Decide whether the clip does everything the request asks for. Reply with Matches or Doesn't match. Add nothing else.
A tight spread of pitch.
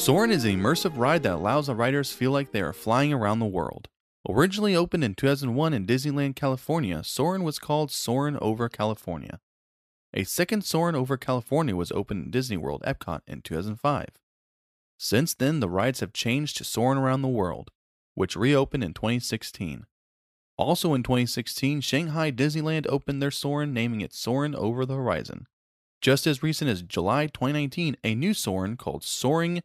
Doesn't match